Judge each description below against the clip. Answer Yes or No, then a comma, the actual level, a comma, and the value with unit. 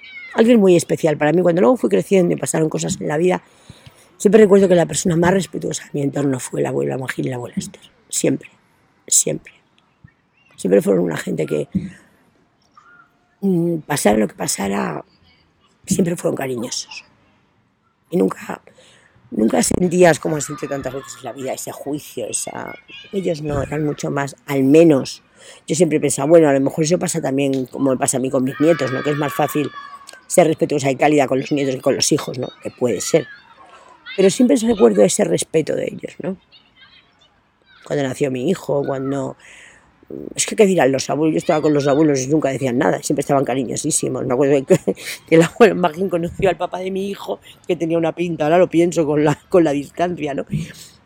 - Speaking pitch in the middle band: Yes, medium, 160 Hz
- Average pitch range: Yes, average, 4.5 semitones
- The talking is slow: No, fast, 190 wpm